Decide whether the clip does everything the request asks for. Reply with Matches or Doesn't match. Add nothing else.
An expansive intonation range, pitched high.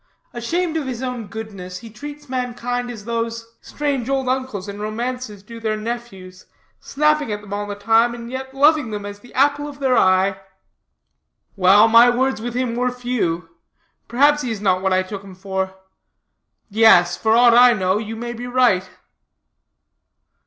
Doesn't match